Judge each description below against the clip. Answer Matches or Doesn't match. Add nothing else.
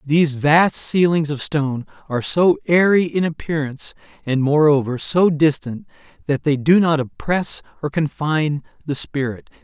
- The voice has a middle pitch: Matches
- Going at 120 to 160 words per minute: Matches